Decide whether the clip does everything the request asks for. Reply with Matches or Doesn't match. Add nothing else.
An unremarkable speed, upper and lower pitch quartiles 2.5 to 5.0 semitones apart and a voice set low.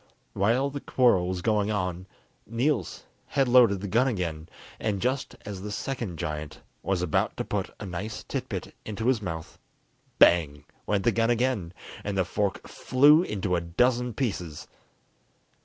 Doesn't match